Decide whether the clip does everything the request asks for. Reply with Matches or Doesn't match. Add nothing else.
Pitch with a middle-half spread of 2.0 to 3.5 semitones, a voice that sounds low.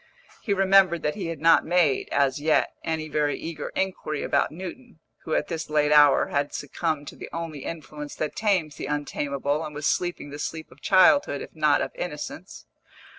Doesn't match